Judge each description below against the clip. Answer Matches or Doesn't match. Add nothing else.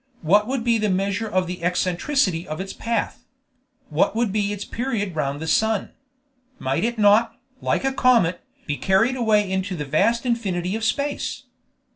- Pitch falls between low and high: Doesn't match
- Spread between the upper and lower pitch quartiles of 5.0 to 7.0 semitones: Doesn't match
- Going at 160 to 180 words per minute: Matches